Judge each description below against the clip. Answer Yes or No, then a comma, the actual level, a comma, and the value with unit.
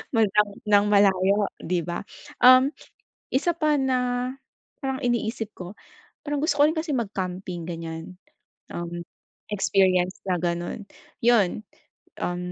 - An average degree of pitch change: No, wide, 6.0 semitones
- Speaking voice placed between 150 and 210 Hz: Yes, high, 205 Hz